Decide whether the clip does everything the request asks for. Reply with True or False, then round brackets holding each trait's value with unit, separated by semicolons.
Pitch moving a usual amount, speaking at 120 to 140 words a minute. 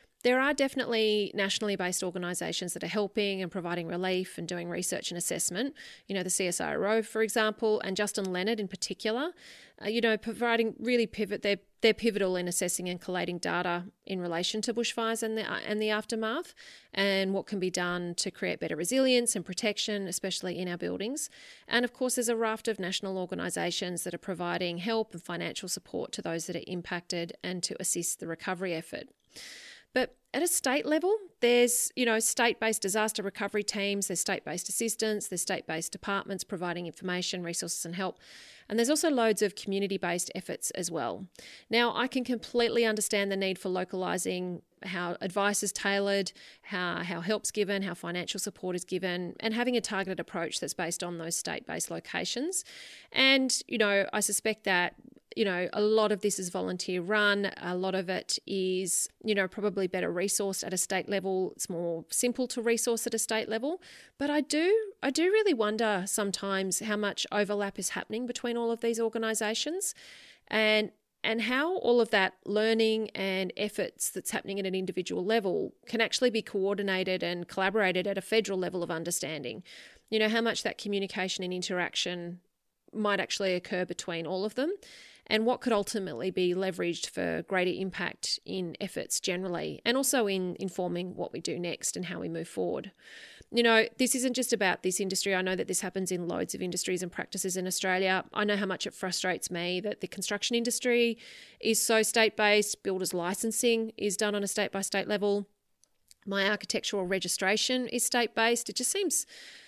False (3.5 semitones; 185 wpm)